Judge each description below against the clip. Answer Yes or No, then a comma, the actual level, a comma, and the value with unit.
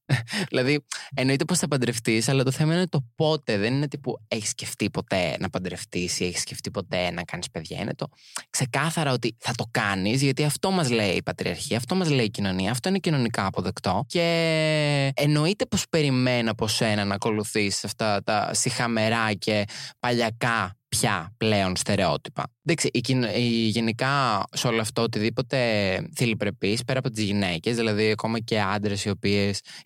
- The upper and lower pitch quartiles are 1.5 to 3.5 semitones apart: No, average, 4.9 semitones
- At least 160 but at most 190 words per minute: Yes, fast, 170 wpm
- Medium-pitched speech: No, low, 120 Hz